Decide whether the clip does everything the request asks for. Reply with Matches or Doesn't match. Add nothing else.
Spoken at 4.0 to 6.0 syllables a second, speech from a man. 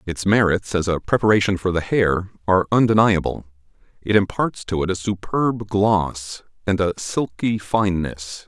Matches